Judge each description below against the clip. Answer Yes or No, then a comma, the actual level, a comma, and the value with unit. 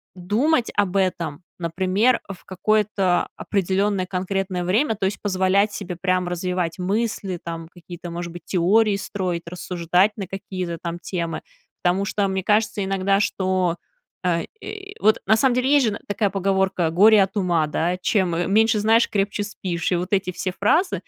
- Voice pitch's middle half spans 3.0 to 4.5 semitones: No, narrow, 2.6 semitones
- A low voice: No, high, 190 Hz